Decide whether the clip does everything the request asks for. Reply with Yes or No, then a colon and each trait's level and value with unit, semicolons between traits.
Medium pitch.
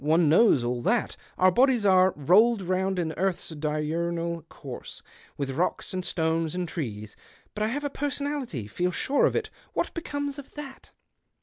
Yes: medium, 180 Hz